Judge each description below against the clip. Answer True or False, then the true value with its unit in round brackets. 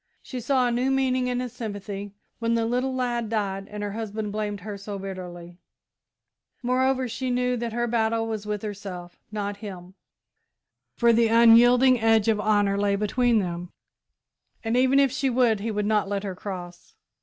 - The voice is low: False (220 Hz)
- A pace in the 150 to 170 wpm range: False (180 wpm)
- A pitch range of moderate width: True (3.3 semitones)